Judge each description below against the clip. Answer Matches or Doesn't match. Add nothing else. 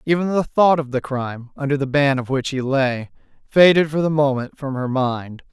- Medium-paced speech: Doesn't match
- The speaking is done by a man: Matches